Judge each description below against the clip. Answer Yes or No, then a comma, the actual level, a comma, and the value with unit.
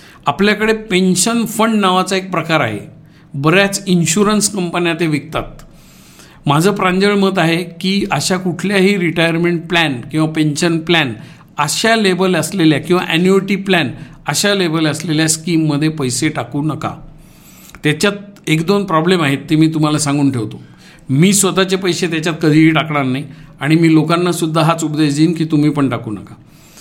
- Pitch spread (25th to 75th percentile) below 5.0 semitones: Yes, average, 3.5 semitones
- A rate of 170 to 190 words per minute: No, average, 150 wpm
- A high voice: No, medium, 165 Hz